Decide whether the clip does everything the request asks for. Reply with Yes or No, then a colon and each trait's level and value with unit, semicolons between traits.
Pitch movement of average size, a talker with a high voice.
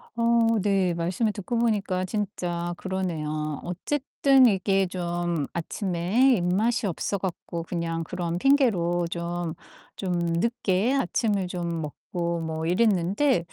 No: average, 3.9 semitones; medium, 180 Hz